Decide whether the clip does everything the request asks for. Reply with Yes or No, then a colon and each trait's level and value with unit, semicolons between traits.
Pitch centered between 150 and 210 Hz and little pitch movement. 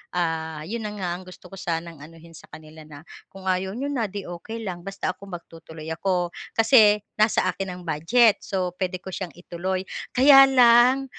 No: medium, 185 Hz; average, 4.0 semitones